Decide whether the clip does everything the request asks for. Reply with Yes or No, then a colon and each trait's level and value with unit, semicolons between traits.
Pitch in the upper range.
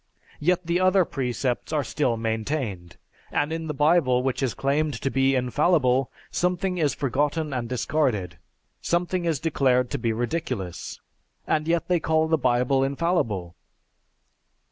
No: medium, 140 Hz